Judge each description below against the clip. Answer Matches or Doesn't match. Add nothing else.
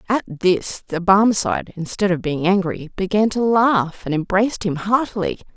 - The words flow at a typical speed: Matches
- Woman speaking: Matches